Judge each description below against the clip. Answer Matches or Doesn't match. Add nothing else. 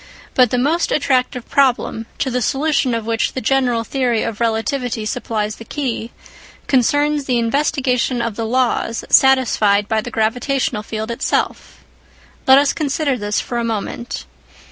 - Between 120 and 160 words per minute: Matches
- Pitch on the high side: Matches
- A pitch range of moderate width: Matches